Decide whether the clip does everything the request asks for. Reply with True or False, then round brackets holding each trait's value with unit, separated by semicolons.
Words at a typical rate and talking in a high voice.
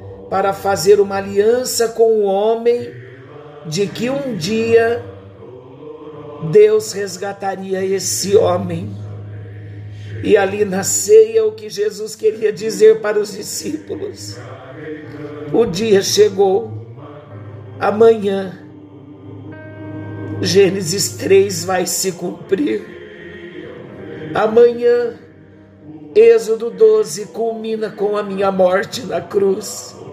False (90 wpm; 195 Hz)